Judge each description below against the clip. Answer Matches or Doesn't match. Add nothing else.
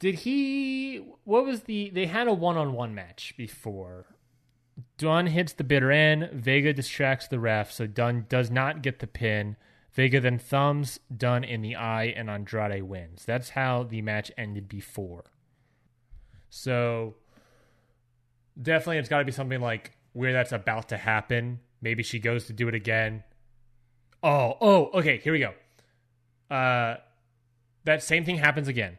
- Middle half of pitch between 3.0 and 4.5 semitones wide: Matches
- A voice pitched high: Doesn't match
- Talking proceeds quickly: Doesn't match